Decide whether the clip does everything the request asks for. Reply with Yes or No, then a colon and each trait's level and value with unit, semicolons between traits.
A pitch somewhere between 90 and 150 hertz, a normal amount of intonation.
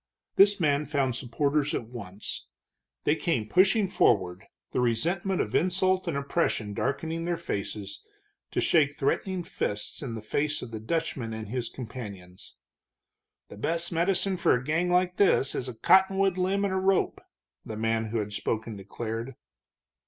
No: medium, 140 Hz; wide, 8.0 semitones